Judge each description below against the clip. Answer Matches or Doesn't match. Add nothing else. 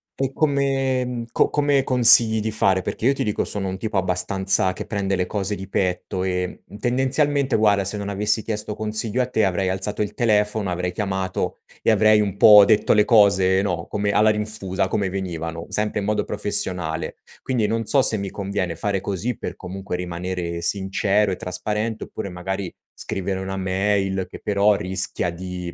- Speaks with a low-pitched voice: Matches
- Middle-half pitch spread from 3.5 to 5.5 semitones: Doesn't match